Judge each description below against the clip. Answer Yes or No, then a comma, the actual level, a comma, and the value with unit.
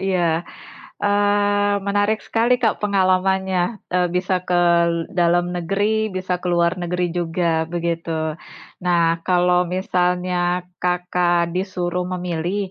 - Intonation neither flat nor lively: No, narrow, 1.6 semitones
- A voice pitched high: No, medium, 180 Hz